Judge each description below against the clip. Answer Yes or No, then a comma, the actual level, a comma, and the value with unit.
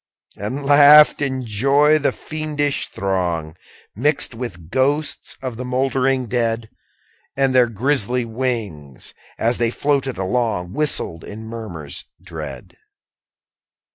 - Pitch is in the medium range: No, low, 125 Hz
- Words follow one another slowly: Yes, slow, 115 wpm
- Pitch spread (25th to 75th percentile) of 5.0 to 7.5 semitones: Yes, average, 5.3 semitones